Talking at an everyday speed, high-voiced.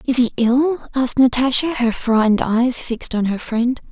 Yes: average, 185 wpm; high, 245 Hz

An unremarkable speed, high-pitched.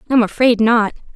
Yes: average, 155 wpm; high, 230 Hz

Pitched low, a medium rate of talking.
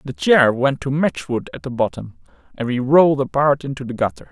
No: low, 130 Hz; fast, 210 wpm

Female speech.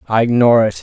No: male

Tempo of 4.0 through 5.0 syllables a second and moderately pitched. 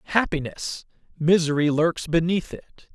Yes: 4.7 syllables/s; medium, 165 Hz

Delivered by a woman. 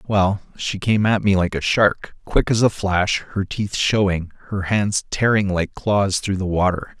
No: male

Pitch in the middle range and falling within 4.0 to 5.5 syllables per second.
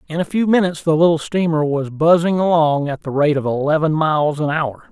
No: medium, 155 Hz; 5.7 syllables/s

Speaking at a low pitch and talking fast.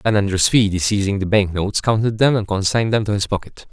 Yes: low, 100 Hz; fast, 225 wpm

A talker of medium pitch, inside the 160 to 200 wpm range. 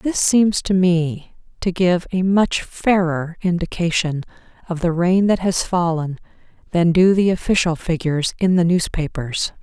No: medium, 175 Hz; average, 150 wpm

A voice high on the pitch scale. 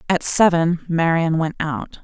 No: medium, 165 Hz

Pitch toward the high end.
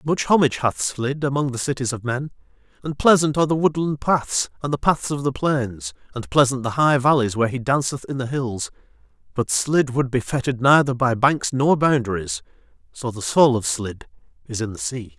No: low, 130 Hz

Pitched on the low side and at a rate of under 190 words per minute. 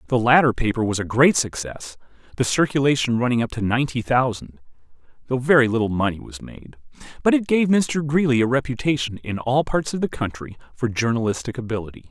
Yes: low, 125 Hz; average, 180 wpm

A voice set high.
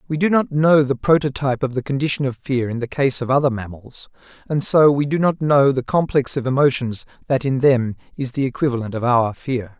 No: low, 135 Hz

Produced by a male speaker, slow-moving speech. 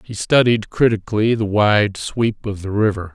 No: male; average, 170 wpm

